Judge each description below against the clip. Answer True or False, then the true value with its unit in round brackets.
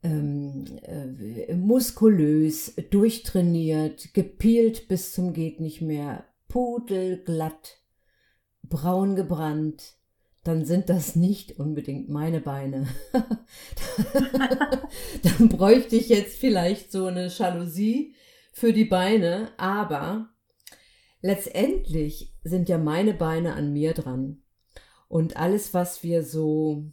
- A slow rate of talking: True (100 wpm)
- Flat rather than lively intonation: False (5.2 semitones)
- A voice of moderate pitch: True (175 Hz)